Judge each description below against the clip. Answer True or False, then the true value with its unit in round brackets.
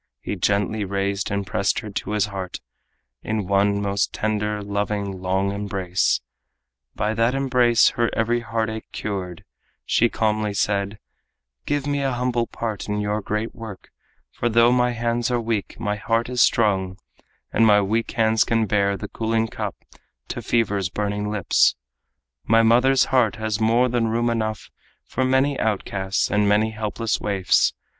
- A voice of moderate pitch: False (110 Hz)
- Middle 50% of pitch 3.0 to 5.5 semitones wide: False (2.5 semitones)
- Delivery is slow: False (155 wpm)